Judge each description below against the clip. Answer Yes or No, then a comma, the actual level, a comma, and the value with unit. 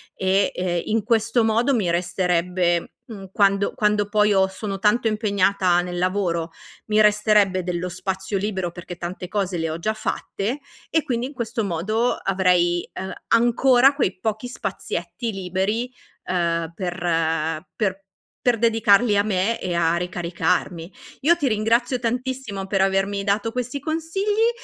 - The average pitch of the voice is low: No, high, 200 Hz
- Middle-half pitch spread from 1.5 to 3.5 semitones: No, average, 4.0 semitones